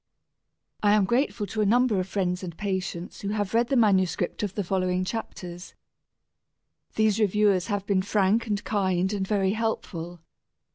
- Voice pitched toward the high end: Yes, high, 200 Hz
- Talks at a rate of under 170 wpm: Yes, average, 160 wpm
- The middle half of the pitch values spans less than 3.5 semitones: Yes, narrow, 2.4 semitones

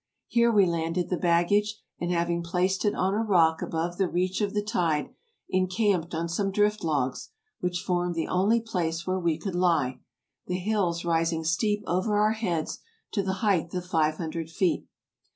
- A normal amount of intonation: Yes, average, 3.3 semitones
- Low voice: No, medium, 180 Hz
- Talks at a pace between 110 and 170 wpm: No, average, 180 wpm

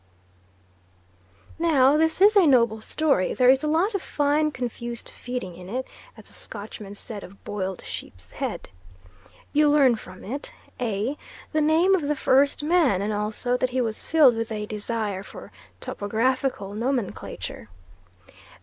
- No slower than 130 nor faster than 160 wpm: Yes, average, 150 wpm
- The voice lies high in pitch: Yes, very high, 250 Hz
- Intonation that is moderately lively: No, wide, 6.0 semitones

